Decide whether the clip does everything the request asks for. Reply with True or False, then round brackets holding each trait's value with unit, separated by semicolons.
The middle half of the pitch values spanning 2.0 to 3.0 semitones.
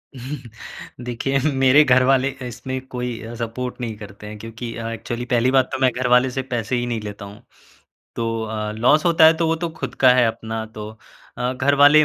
True (2.7 semitones)